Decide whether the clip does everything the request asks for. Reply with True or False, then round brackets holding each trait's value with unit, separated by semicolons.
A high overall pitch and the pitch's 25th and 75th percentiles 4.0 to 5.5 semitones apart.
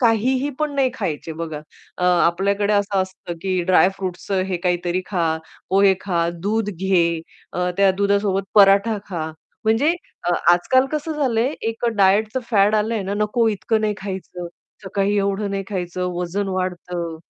False (195 Hz; 2.9 semitones)